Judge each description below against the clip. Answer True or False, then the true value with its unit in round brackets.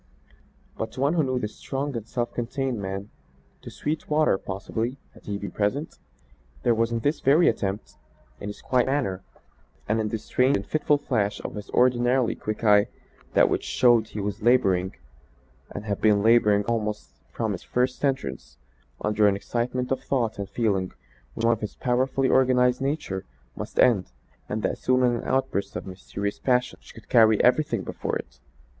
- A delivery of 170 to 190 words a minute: True (180 wpm)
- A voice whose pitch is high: False (115 Hz)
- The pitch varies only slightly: False (3.9 semitones)